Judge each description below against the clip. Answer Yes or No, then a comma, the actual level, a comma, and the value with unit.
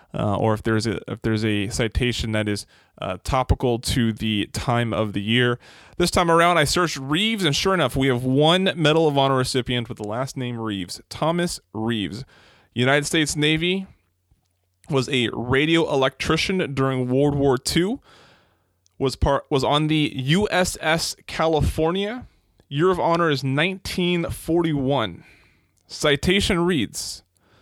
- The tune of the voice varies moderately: No, wide, 6.4 semitones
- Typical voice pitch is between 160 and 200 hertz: No, low, 135 Hz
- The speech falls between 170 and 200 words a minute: No, average, 145 wpm